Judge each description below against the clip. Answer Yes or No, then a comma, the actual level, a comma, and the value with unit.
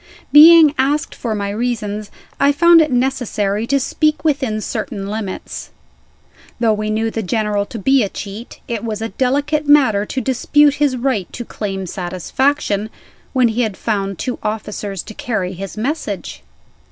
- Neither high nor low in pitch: No, high, 225 Hz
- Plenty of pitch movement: No, average, 4.8 semitones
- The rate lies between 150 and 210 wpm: Yes, average, 160 wpm